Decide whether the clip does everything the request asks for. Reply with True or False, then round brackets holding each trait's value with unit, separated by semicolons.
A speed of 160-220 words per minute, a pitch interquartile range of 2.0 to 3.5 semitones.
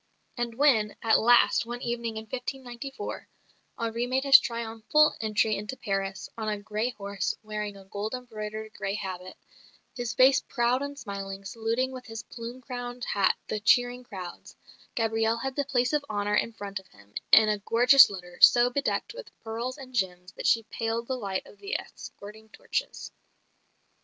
True (170 wpm; 3.1 semitones)